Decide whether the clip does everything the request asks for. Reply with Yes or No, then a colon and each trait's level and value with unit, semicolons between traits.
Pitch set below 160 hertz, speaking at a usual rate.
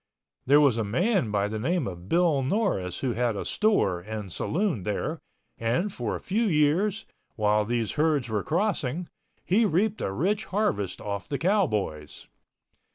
Yes: medium, 140 Hz; average, 160 wpm